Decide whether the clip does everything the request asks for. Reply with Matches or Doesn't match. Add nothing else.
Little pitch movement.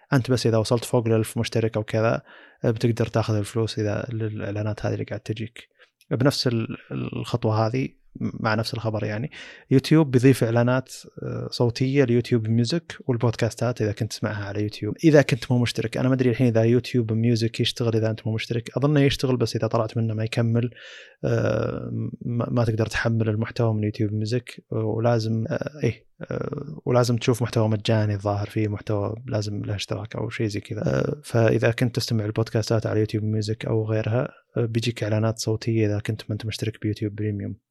Matches